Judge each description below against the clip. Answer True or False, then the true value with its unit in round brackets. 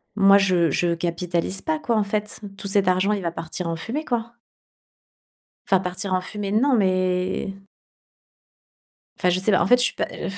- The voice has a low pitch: False (190 Hz)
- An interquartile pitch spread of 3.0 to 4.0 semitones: False (2.6 semitones)